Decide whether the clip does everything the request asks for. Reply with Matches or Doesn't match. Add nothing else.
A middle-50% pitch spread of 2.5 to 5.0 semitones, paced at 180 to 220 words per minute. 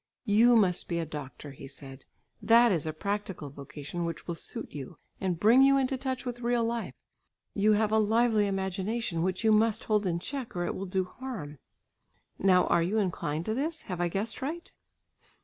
Doesn't match